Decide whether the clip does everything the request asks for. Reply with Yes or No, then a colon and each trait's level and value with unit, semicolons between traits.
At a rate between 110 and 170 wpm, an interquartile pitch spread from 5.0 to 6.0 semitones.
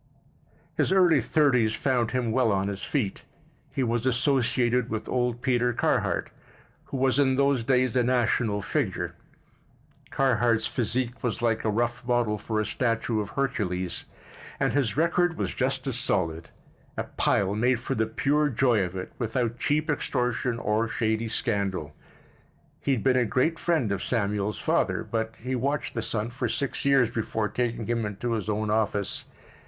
No: average, 165 wpm; average, 3.1 semitones